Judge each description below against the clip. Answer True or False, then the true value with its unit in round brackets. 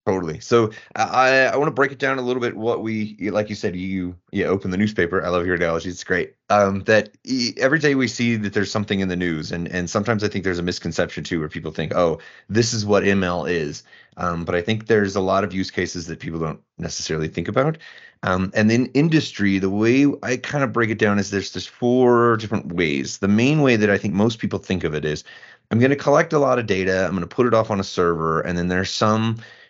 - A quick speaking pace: True (255 wpm)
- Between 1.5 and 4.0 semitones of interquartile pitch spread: False (4.7 semitones)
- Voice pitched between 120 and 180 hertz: False (105 Hz)